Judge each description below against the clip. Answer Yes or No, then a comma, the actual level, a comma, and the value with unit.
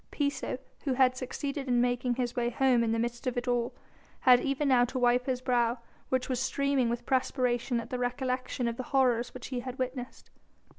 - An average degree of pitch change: No, narrow, 1.2 semitones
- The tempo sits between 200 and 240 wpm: Yes, fast, 205 wpm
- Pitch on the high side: Yes, very high, 250 Hz